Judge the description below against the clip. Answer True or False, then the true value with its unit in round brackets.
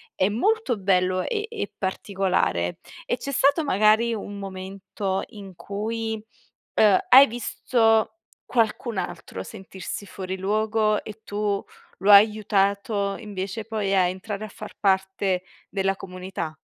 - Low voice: False (200 Hz)